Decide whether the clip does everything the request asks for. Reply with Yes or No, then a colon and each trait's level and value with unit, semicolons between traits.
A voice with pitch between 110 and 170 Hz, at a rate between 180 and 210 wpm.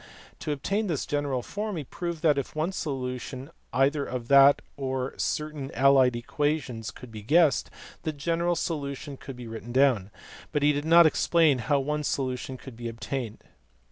No: medium, 140 Hz; average, 170 wpm